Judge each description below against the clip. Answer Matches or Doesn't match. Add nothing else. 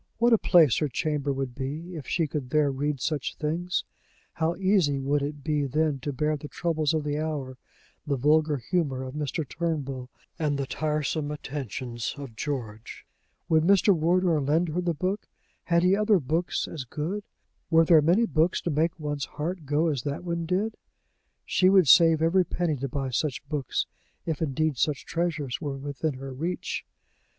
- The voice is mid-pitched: Matches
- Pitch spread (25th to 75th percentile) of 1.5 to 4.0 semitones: Matches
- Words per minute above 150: Matches